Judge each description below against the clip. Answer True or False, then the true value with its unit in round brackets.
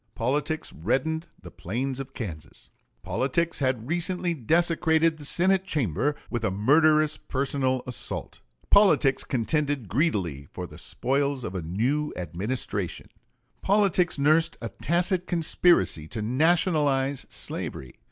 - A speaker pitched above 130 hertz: True (140 Hz)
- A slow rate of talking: True (120 wpm)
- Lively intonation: True (6.0 semitones)